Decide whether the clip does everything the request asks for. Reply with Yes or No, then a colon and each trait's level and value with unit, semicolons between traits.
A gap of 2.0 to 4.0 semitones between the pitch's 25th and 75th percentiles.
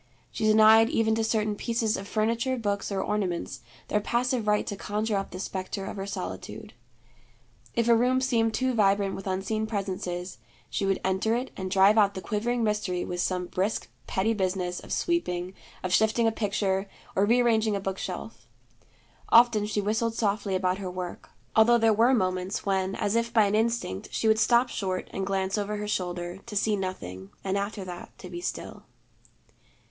Yes: average, 2.9 semitones